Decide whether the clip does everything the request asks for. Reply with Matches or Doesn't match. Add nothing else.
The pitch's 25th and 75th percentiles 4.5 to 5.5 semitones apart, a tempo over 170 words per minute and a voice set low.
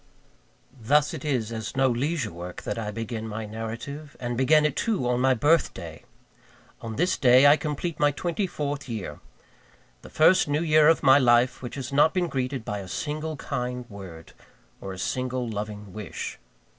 Matches